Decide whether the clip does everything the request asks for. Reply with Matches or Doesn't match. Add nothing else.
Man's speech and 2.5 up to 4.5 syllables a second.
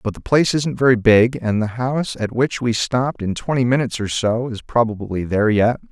Doesn't match